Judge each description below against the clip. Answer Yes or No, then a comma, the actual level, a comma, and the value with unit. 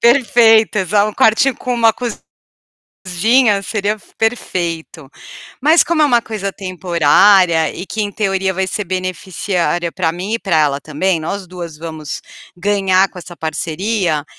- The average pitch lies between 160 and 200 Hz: Yes, high, 190 Hz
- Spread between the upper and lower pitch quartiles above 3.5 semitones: Yes, average, 4.0 semitones